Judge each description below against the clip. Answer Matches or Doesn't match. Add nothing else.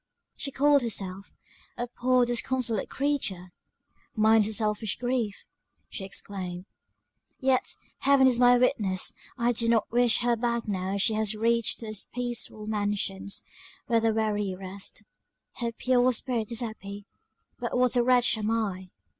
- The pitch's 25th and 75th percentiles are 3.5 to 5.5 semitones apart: Doesn't match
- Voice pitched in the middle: Doesn't match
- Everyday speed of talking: Matches